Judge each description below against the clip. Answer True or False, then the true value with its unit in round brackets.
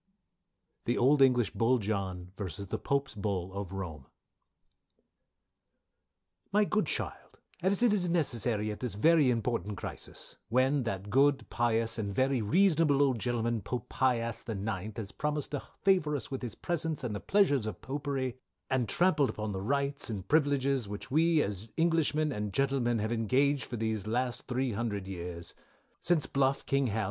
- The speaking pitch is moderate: False (125 Hz)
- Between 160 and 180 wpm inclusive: True (165 wpm)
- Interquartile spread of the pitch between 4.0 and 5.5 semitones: True (5.2 semitones)